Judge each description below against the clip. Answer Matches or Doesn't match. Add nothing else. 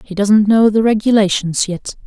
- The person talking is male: Doesn't match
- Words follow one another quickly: Doesn't match